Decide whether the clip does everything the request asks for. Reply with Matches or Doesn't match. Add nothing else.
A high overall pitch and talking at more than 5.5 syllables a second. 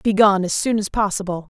Matches